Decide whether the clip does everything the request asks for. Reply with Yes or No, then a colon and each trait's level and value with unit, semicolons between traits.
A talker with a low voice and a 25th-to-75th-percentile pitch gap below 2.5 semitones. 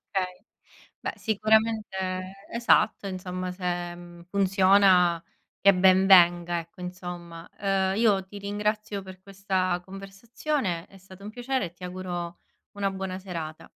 No: high, 190 Hz; narrow, 1.8 semitones